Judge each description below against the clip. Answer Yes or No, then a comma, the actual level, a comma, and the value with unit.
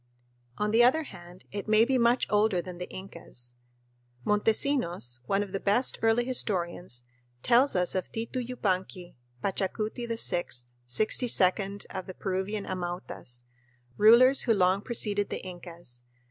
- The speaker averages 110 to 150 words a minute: Yes, average, 140 wpm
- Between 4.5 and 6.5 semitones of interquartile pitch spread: No, average, 4.1 semitones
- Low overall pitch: No, high, 200 Hz